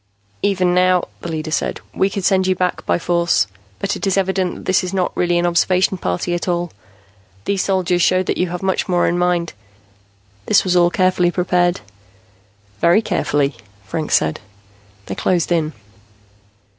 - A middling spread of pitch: No, narrow, 1.4 semitones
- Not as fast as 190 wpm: Yes, average, 170 wpm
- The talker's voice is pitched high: No, medium, 180 Hz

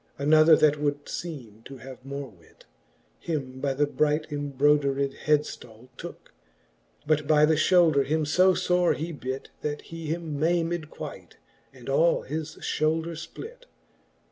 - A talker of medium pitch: Yes, medium, 150 Hz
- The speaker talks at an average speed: Yes, average, 145 wpm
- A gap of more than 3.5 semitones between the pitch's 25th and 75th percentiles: No, narrow, 2.6 semitones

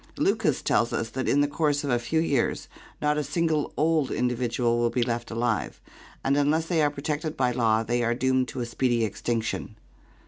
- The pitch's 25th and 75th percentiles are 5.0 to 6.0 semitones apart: No, average, 3.8 semitones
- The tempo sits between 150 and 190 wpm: No, average, 200 wpm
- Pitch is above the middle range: No, low, 130 Hz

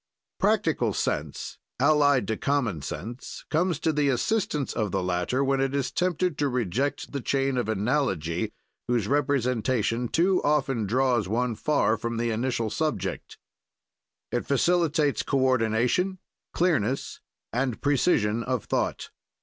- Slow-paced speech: Yes, slow, 130 wpm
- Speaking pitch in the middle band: No, low, 130 Hz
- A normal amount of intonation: Yes, average, 4.2 semitones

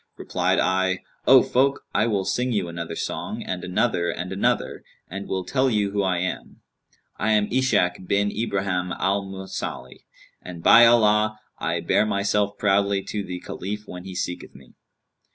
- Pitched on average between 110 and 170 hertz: No, low, 100 Hz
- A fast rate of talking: No, average, 165 wpm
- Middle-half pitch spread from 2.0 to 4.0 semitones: Yes, average, 2.7 semitones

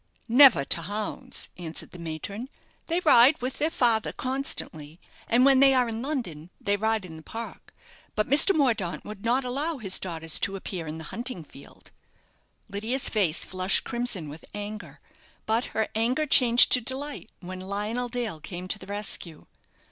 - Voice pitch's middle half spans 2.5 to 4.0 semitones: No, wide, 5.6 semitones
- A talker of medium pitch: No, high, 220 Hz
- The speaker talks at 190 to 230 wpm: No, average, 170 wpm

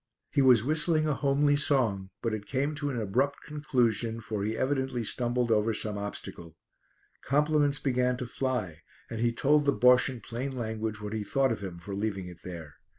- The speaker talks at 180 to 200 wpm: Yes, average, 190 wpm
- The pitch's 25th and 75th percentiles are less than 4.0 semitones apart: No, average, 4.5 semitones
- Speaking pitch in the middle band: No, low, 120 Hz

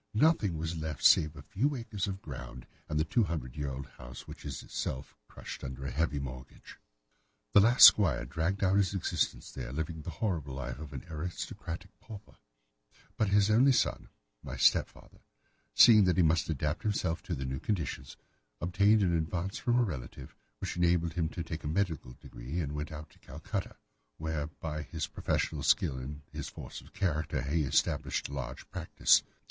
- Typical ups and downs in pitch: Yes, average, 5.0 semitones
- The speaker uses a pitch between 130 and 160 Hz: No, very low, 80 Hz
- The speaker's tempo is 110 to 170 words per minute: No, average, 185 wpm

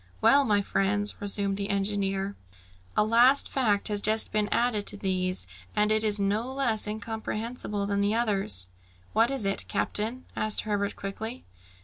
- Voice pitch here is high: Yes, high, 210 Hz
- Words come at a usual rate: Yes, average, 155 wpm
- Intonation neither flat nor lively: No, narrow, 1.9 semitones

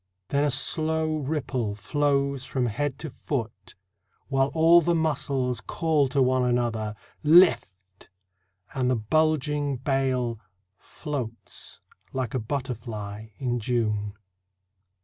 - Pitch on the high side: No, low, 130 Hz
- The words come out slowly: Yes, slow, 115 wpm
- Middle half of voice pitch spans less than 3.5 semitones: No, average, 4.1 semitones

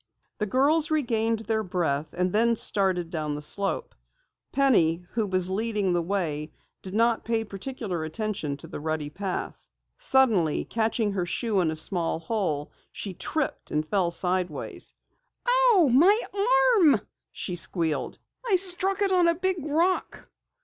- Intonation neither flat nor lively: No, wide, 8.4 semitones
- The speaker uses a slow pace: No, average, 150 wpm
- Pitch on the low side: No, high, 210 Hz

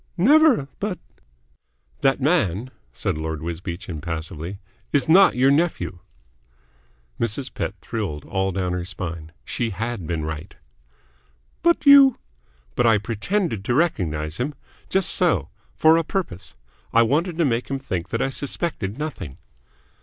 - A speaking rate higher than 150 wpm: No, average, 145 wpm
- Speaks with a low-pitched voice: Yes, low, 115 Hz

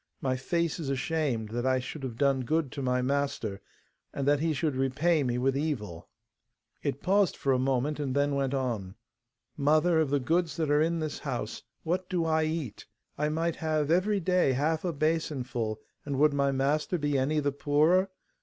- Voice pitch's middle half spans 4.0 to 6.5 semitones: No, average, 3.3 semitones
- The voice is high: No, medium, 145 Hz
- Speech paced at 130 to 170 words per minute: No, average, 190 wpm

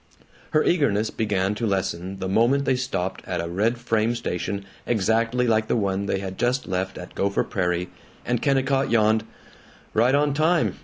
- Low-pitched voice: Yes, low, 110 Hz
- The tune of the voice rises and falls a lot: No, average, 4.4 semitones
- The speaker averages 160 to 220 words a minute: Yes, average, 170 wpm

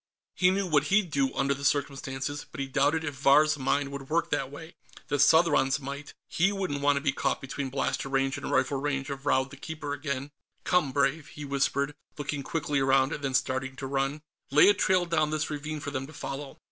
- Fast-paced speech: Yes, fast, 215 wpm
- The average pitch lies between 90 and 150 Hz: Yes, medium, 140 Hz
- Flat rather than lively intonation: Yes, narrow, 2.0 semitones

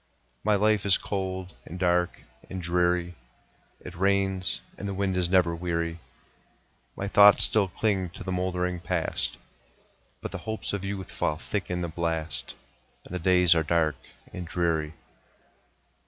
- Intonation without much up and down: Yes, narrow, 2.2 semitones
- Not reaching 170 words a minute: Yes, average, 155 wpm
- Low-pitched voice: Yes, very low, 90 Hz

